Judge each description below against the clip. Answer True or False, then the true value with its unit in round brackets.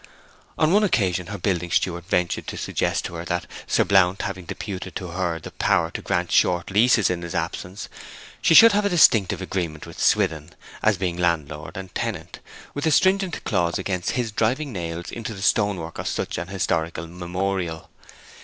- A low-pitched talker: True (90 Hz)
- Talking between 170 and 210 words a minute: True (180 wpm)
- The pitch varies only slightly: False (3.7 semitones)